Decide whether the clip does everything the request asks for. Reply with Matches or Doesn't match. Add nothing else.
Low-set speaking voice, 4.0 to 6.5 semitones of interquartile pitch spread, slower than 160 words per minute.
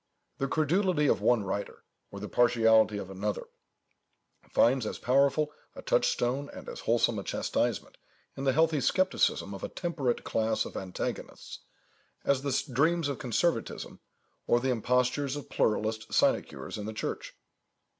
Matches